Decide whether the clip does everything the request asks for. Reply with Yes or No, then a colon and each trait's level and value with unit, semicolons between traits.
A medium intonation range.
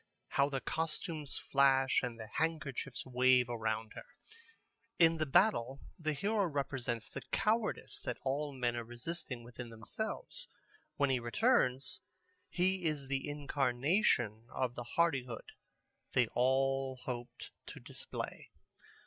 Yes: average, 4.4 semitones